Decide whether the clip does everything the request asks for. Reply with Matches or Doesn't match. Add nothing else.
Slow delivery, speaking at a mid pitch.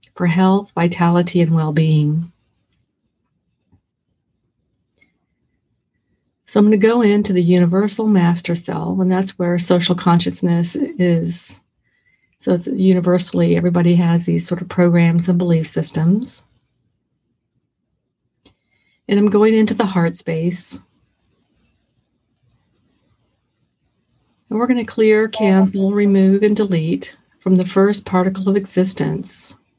Matches